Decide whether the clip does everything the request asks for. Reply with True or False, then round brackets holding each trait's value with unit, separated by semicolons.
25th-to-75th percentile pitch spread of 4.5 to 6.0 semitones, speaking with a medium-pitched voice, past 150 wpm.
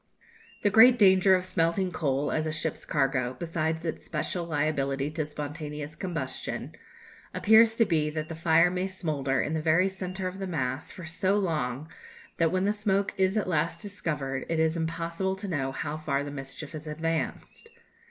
False (3.8 semitones; 160 Hz; 180 wpm)